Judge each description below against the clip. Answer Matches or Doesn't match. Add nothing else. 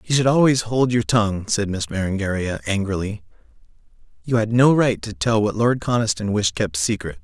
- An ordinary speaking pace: Matches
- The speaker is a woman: Doesn't match